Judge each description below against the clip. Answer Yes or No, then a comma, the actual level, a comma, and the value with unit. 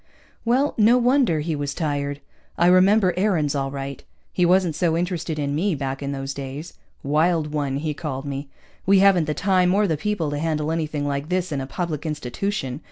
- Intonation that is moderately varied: Yes, average, 4.3 semitones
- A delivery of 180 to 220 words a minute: Yes, average, 195 wpm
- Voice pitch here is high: No, medium, 155 Hz